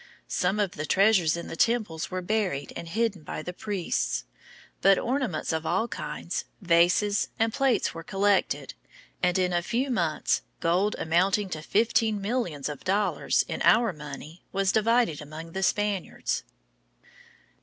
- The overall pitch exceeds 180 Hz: Yes, high, 190 Hz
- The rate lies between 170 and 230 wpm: No, average, 150 wpm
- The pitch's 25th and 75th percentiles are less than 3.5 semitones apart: No, average, 4.4 semitones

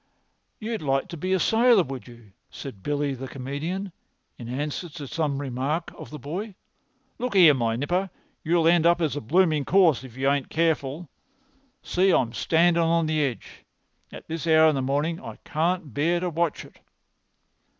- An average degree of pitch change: Yes, average, 4.1 semitones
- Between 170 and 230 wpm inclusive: Yes, average, 180 wpm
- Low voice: No, medium, 155 Hz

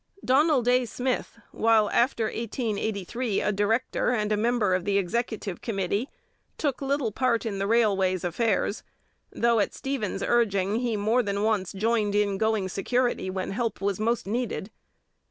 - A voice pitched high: Yes, high, 220 Hz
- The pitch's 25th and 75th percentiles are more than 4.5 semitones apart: No, average, 3.2 semitones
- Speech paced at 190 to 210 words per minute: No, average, 155 wpm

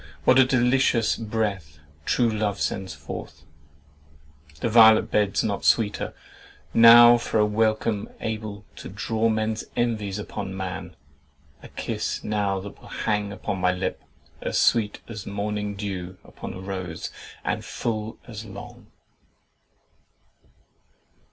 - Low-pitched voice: Yes, low, 105 Hz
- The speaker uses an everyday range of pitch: No, narrow, 2.2 semitones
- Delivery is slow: Yes, slow, 125 wpm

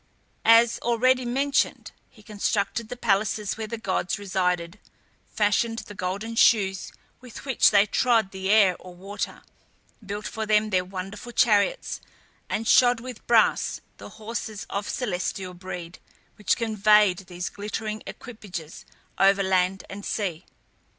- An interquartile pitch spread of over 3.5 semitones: No, average, 3.1 semitones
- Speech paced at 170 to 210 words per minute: No, slow, 135 wpm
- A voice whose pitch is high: Yes, high, 210 Hz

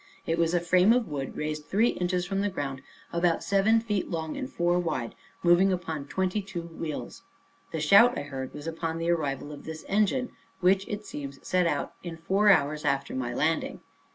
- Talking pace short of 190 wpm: No, average, 195 wpm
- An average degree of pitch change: Yes, average, 4.3 semitones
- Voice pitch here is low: No, medium, 170 Hz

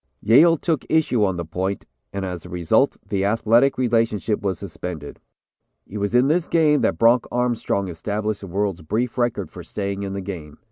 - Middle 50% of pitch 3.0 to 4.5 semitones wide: Yes, average, 4.2 semitones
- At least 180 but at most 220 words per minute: Yes, average, 185 wpm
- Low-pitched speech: Yes, low, 105 Hz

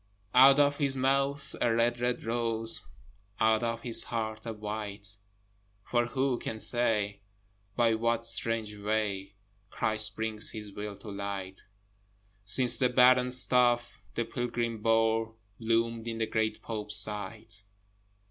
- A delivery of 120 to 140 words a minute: Yes, slow, 135 wpm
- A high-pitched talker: No, low, 115 Hz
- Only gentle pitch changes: Yes, narrow, 2.1 semitones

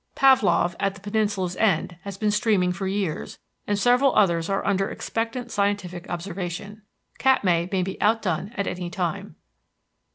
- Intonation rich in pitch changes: No, average, 2.8 semitones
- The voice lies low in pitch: No, high, 195 Hz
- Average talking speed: Yes, average, 150 wpm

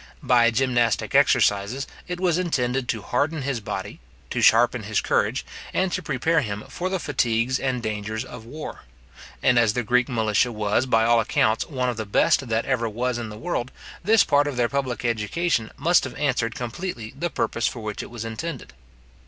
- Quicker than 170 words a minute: Yes, average, 190 wpm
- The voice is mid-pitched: No, low, 120 Hz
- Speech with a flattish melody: No, average, 3.7 semitones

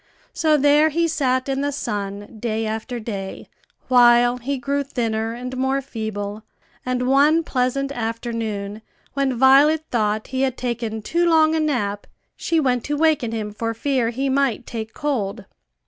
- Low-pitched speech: No, very high, 250 Hz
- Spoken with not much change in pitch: No, average, 3.9 semitones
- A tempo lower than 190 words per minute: Yes, average, 160 wpm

